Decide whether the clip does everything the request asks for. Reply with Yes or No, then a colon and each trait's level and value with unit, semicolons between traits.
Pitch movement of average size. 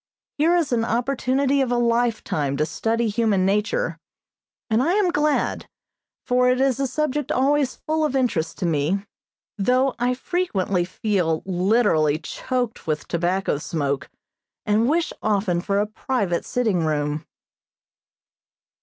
No: wide, 6.7 semitones